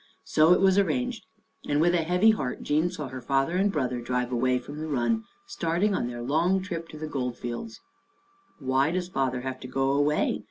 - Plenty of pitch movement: Yes, wide, 5.8 semitones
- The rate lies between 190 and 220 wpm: Yes, fast, 205 wpm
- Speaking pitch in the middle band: Yes, medium, 150 Hz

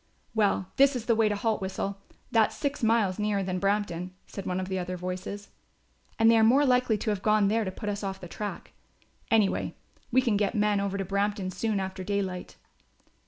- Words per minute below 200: No, fast, 205 wpm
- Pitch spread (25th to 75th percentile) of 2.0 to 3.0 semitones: Yes, average, 2.7 semitones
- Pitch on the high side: Yes, high, 205 Hz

